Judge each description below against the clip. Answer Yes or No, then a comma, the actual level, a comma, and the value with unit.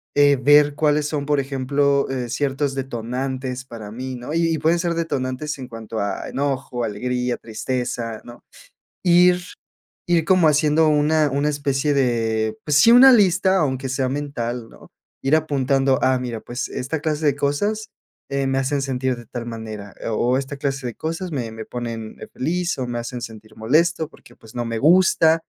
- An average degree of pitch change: Yes, average, 3.6 semitones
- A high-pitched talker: No, low, 135 Hz